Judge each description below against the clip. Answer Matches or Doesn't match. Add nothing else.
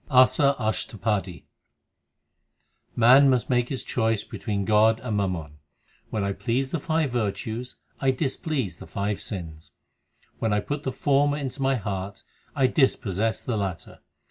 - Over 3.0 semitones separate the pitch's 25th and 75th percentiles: Matches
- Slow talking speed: Doesn't match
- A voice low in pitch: Matches